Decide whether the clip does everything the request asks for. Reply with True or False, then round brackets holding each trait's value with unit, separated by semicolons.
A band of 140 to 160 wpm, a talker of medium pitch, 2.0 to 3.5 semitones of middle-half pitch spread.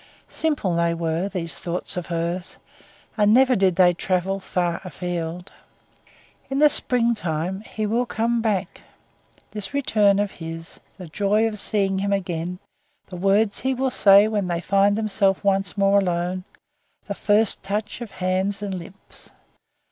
False (150 wpm; 195 Hz; 3.0 semitones)